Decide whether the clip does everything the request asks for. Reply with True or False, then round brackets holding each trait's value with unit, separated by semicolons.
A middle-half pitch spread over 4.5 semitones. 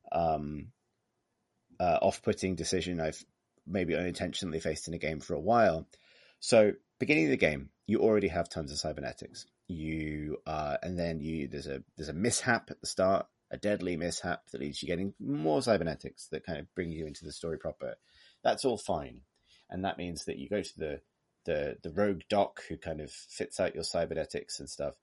False (2.7 semitones)